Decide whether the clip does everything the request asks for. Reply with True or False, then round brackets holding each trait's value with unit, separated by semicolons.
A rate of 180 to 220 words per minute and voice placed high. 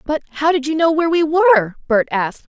False (235 wpm; 300 Hz)